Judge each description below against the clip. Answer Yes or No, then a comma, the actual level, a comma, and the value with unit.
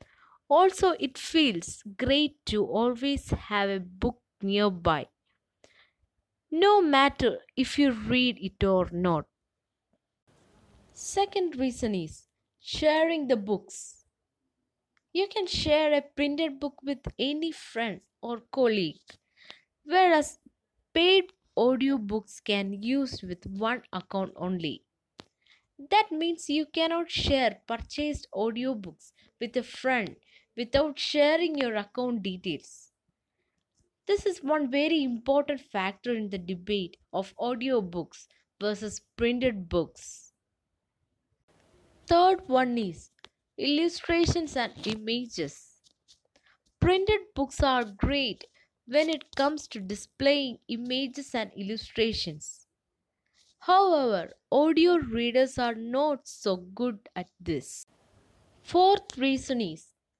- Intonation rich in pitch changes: Yes, wide, 6.5 semitones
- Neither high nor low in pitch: No, very high, 255 Hz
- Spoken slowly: Yes, slow, 105 wpm